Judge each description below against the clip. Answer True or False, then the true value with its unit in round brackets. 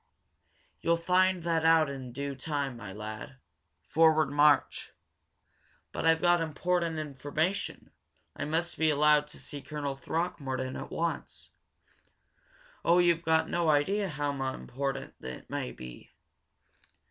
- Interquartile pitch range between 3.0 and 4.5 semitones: True (3.4 semitones)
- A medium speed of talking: False (125 wpm)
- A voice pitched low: False (150 Hz)